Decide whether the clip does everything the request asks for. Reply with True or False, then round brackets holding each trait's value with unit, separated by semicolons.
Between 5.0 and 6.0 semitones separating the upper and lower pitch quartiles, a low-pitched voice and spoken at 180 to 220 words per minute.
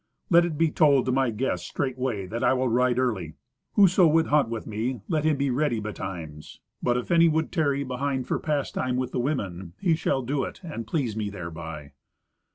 True (5.4 semitones; 130 Hz; 200 wpm)